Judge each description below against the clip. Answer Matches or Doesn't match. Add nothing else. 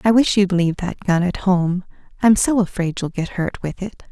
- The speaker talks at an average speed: Doesn't match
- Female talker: Matches